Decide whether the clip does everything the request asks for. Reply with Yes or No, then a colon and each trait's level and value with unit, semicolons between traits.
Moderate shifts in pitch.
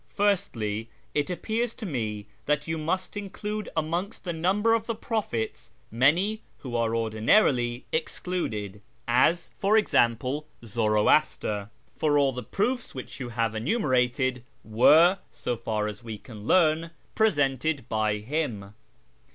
No: wide, 8.4 semitones